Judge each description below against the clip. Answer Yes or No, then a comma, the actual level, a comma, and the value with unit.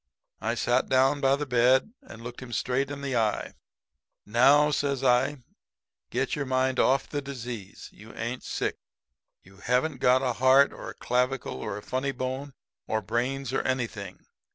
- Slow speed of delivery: No, average, 170 wpm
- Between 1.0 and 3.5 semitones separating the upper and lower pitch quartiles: Yes, narrow, 2.4 semitones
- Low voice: Yes, low, 130 Hz